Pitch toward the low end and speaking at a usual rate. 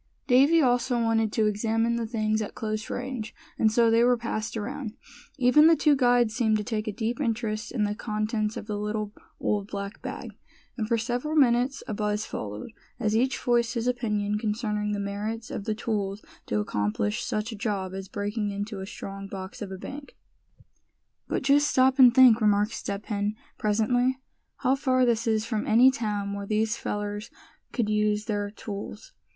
No: high, 220 Hz; average, 185 wpm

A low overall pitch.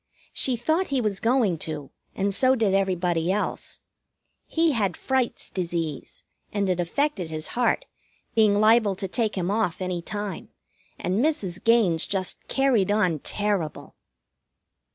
No: high, 200 Hz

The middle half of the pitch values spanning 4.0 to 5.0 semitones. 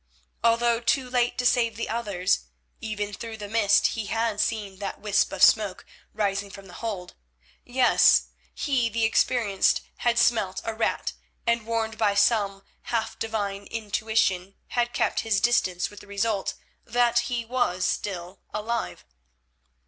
No: average, 2.7 semitones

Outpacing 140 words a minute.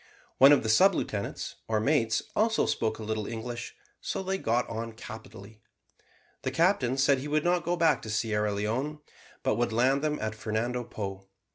Yes: average, 180 wpm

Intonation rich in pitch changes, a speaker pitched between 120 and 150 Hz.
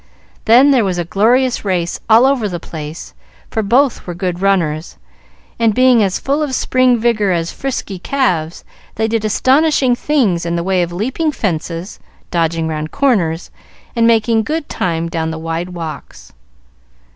No: wide, 6.7 semitones; high, 200 Hz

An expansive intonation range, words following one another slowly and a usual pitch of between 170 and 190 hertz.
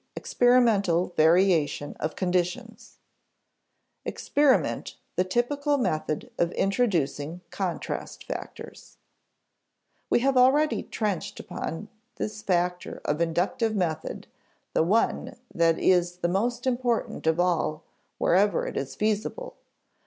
Yes: wide, 6.1 semitones; slow, 110 wpm; medium, 185 Hz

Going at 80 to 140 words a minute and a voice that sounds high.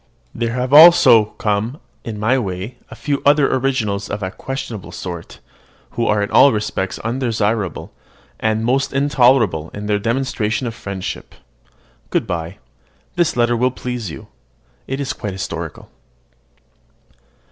No: slow, 135 wpm; low, 115 Hz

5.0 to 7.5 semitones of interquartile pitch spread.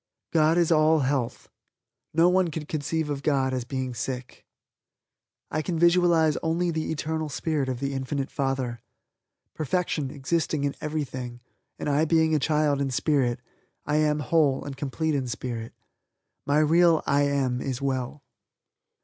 No: average, 3.1 semitones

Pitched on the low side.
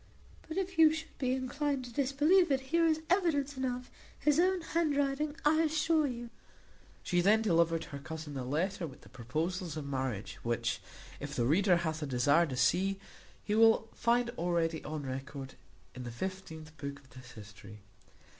No: high, 190 Hz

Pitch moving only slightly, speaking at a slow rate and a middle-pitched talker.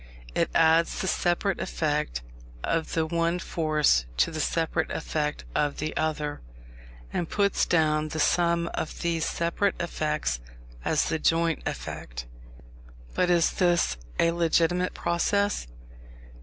Yes: narrow, 2.0 semitones; slow, 130 wpm; medium, 165 Hz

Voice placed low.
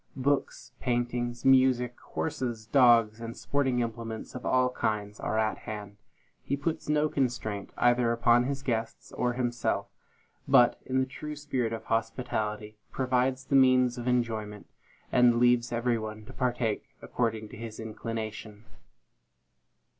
Yes: low, 120 Hz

